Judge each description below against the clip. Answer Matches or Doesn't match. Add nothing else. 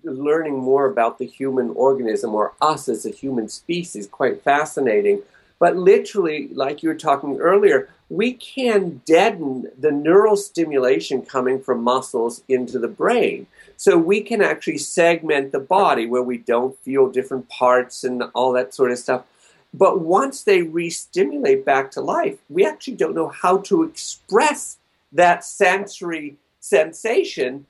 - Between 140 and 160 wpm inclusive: Matches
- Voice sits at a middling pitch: Matches